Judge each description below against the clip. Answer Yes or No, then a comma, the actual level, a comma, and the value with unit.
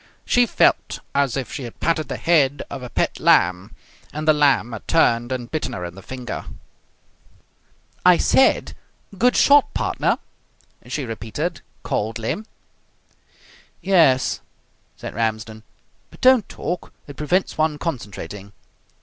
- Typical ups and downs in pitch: No, wide, 6.4 semitones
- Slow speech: Yes, slow, 130 wpm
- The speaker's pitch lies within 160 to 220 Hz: No, low, 135 Hz